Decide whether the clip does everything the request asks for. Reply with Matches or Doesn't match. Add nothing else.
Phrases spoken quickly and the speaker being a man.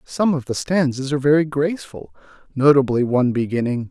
Doesn't match